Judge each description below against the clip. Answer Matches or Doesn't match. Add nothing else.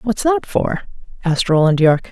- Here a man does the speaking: Doesn't match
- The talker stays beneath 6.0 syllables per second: Matches